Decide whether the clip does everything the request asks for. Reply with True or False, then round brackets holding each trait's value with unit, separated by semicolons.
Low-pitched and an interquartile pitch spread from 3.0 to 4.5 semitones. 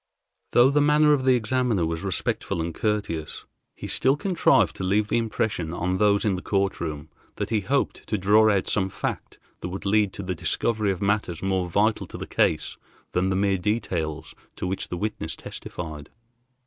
True (100 Hz; 3.4 semitones)